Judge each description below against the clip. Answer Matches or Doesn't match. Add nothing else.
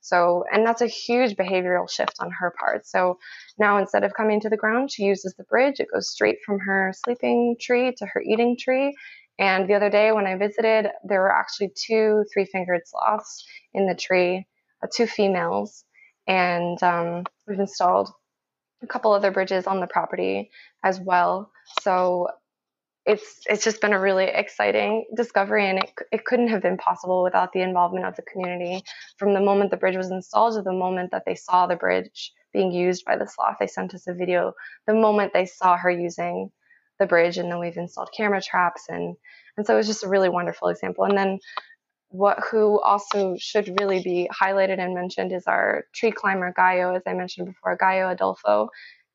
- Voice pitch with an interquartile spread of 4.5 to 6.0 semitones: Doesn't match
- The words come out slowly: Doesn't match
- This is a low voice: Doesn't match